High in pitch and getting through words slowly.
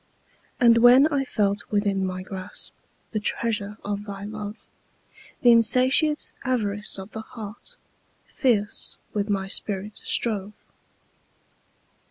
Yes: high, 210 Hz; slow, 110 wpm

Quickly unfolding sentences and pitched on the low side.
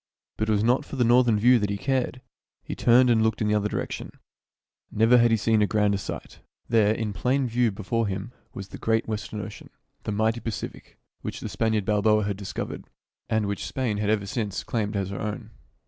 Yes: fast, 210 wpm; low, 110 Hz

